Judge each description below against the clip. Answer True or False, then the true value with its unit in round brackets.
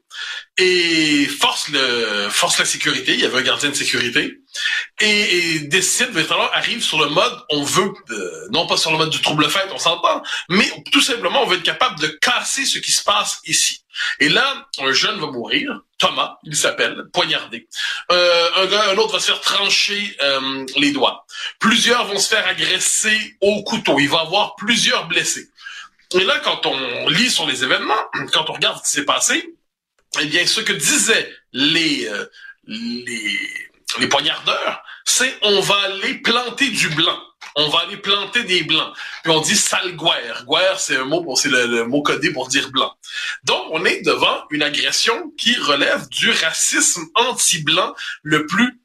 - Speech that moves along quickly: False (185 wpm)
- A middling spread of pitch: False (8.4 semitones)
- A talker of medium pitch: False (215 Hz)